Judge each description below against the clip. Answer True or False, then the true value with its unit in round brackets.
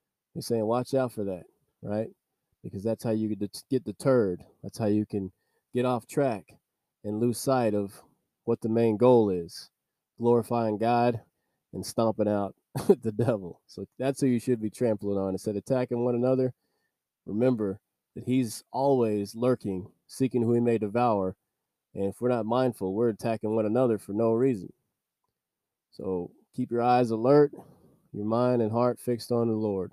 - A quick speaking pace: False (170 wpm)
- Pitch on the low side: True (115 Hz)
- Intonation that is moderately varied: True (3.0 semitones)